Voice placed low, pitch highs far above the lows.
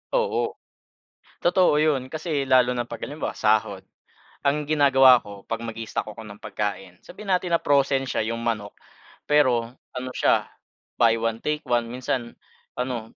No: low, 125 Hz; average, 4.1 semitones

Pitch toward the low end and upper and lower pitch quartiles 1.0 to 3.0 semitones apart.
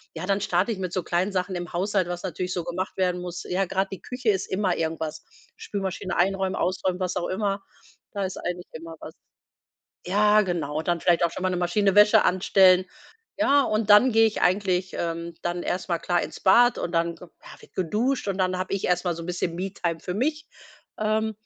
No: medium, 185 Hz; narrow, 2.4 semitones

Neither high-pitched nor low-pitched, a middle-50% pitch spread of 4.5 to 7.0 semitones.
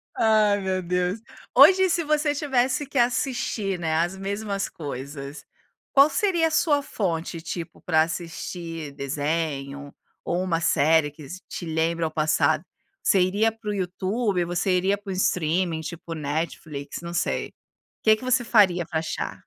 Yes: medium, 180 Hz; average, 5.2 semitones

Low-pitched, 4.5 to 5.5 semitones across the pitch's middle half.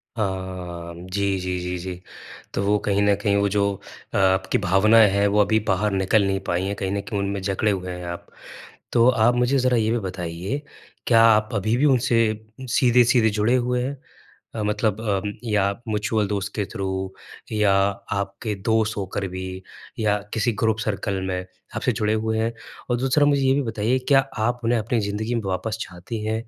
No: low, 105 Hz; average, 2.8 semitones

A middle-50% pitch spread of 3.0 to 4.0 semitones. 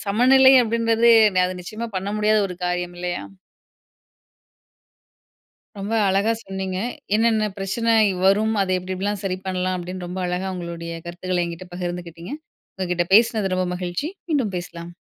Yes: average, 3.3 semitones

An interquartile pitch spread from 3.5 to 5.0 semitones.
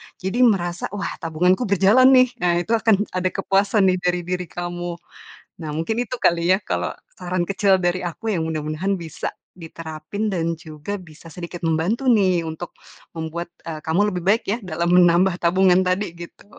No: average, 2.7 semitones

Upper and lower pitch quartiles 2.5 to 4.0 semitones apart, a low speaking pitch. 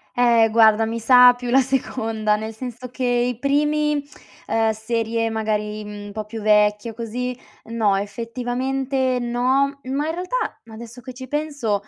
No: average, 2.9 semitones; high, 235 Hz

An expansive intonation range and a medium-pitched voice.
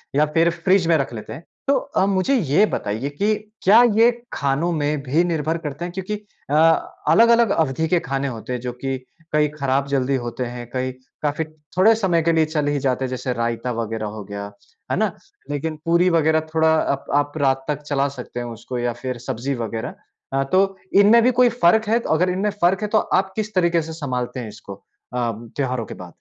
Yes: wide, 5.8 semitones; medium, 145 Hz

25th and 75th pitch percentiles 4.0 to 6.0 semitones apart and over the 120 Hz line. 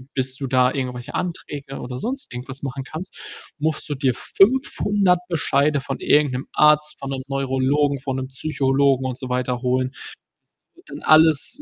No: average, 2.8 semitones; low, 135 Hz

